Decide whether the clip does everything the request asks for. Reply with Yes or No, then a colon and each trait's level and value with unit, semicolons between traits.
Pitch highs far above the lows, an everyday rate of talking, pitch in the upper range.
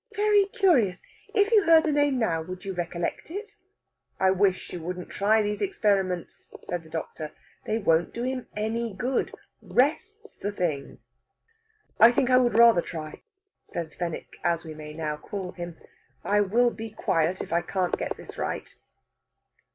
Yes: wide, 6.5 semitones; average, 165 wpm; high, 200 Hz